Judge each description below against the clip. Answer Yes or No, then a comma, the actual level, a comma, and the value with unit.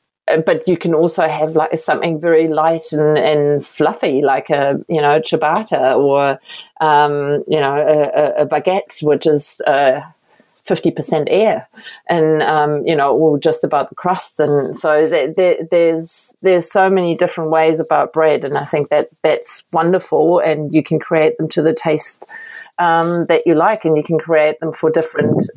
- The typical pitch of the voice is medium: Yes, medium, 160 Hz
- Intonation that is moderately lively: No, narrow, 1.8 semitones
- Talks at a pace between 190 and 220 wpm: No, average, 180 wpm